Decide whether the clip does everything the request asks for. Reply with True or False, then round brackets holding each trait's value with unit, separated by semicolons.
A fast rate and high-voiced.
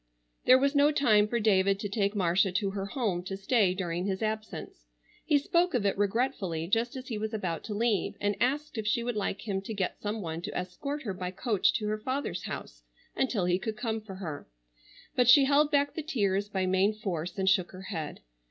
True (220 wpm; 205 Hz)